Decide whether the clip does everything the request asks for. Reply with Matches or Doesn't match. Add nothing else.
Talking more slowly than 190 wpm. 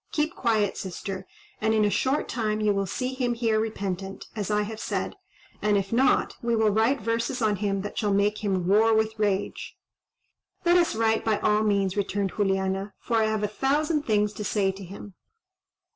Doesn't match